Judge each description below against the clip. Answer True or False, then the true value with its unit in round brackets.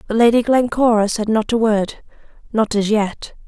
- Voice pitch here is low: False (220 Hz)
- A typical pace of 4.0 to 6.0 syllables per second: True (4.8 syllables/s)